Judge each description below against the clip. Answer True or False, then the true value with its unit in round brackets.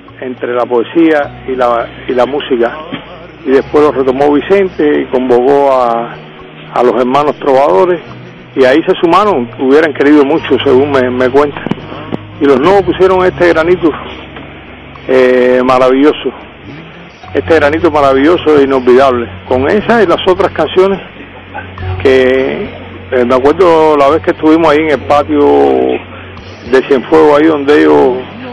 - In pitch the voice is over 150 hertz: False (135 Hz)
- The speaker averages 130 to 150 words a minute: True (140 wpm)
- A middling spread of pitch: True (3.6 semitones)